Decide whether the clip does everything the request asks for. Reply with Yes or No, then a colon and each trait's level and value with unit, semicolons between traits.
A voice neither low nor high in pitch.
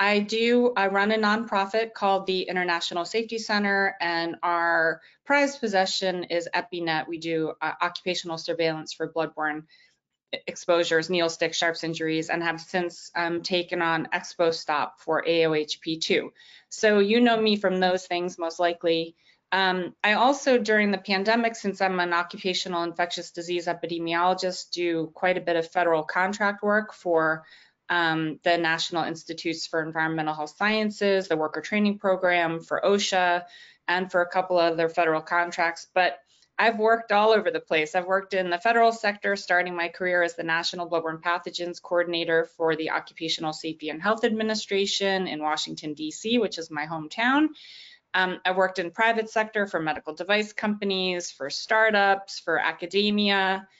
Yes: medium, 175 Hz